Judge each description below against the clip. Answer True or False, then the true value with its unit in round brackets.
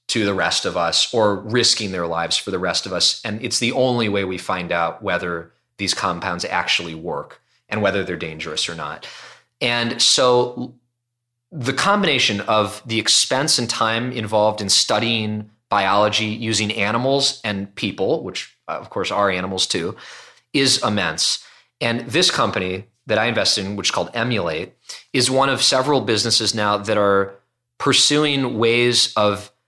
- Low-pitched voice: True (110 Hz)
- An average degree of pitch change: True (3.3 semitones)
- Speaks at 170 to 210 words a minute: False (160 wpm)